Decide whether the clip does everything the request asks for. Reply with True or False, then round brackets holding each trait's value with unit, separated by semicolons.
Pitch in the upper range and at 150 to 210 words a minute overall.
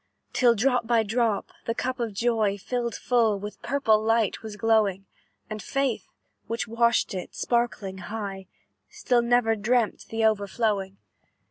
False (225 Hz; 140 wpm)